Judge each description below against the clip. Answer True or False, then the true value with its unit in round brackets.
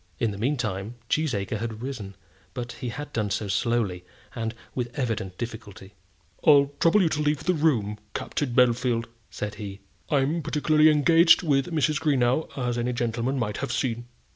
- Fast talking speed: False (165 wpm)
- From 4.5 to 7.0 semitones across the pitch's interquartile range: True (4.9 semitones)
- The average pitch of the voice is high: False (120 Hz)